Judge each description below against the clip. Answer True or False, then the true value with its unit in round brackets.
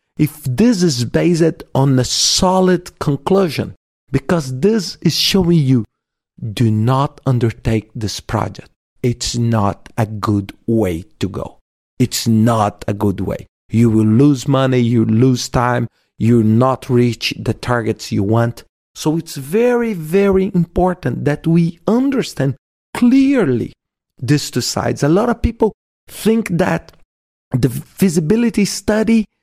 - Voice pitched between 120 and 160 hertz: True (135 Hz)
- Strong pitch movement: True (7.7 semitones)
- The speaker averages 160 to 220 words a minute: False (135 wpm)